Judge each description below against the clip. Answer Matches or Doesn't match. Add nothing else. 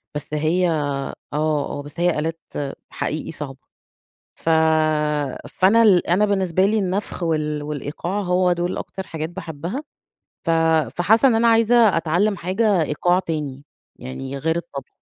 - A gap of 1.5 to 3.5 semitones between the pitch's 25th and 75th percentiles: Doesn't match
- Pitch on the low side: Doesn't match